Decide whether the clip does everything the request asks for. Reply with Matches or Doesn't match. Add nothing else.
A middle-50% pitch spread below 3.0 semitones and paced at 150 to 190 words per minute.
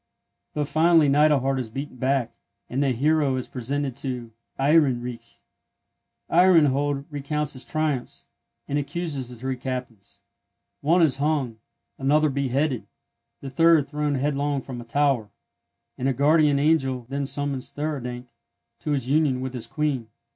Doesn't match